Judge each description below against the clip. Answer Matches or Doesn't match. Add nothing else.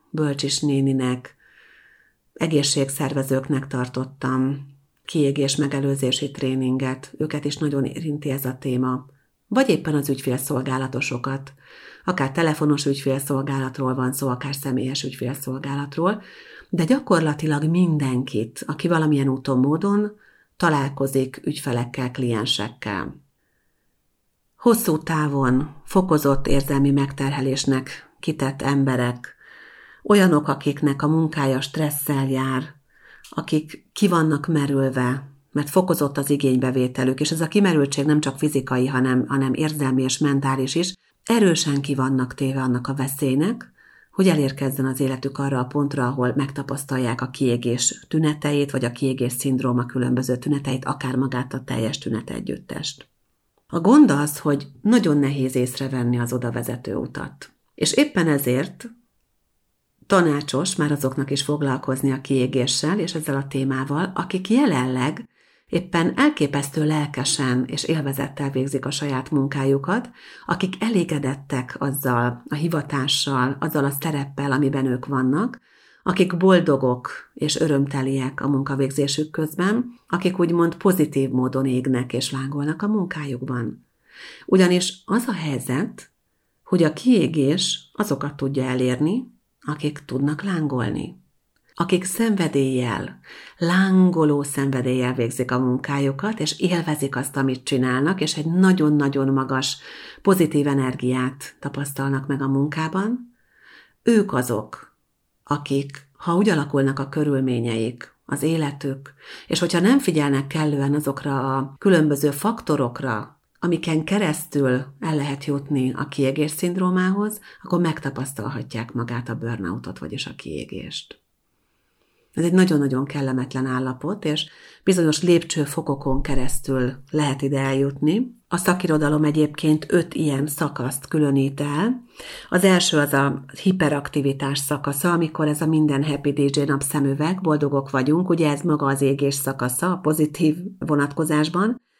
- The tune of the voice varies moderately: Matches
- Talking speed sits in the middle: Matches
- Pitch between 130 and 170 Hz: Matches